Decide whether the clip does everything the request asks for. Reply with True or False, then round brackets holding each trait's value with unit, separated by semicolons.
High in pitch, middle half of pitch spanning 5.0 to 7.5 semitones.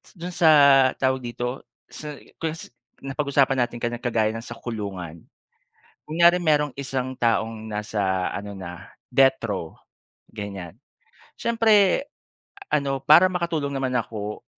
False (125 Hz; 5.6 semitones)